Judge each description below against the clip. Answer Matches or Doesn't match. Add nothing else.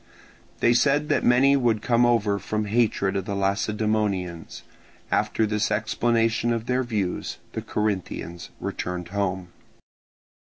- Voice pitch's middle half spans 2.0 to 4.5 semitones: Matches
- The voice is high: Doesn't match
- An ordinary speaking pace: Doesn't match